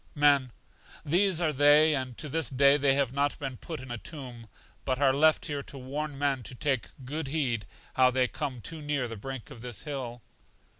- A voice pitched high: No, medium, 140 Hz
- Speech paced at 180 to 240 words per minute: Yes, fast, 205 wpm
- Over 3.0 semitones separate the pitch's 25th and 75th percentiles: No, narrow, 2.6 semitones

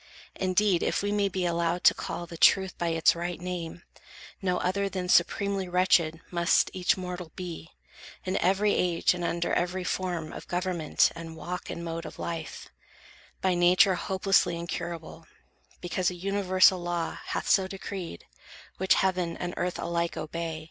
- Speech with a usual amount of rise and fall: No, narrow, 1.7 semitones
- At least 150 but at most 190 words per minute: Yes, average, 160 wpm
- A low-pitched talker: No, medium, 180 Hz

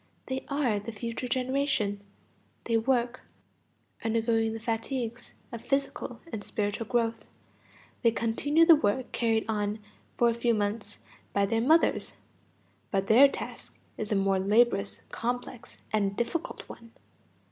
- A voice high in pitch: Yes, high, 230 Hz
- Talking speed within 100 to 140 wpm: Yes, slow, 135 wpm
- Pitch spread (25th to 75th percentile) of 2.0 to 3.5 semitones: Yes, average, 2.8 semitones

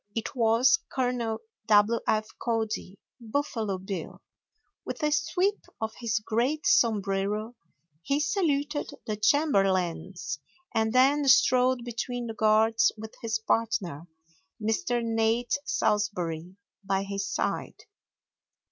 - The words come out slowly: Yes, slow, 110 wpm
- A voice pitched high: Yes, high, 225 Hz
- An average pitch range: Yes, average, 3.3 semitones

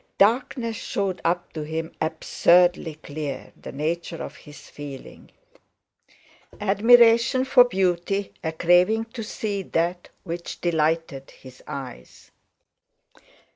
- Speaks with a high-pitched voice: No, medium, 175 Hz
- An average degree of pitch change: Yes, average, 4.6 semitones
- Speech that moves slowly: Yes, slow, 100 wpm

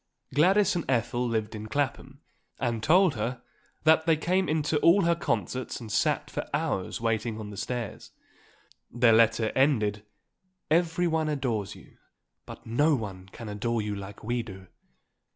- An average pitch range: No, wide, 6.2 semitones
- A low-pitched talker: Yes, low, 120 Hz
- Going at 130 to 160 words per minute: Yes, average, 155 wpm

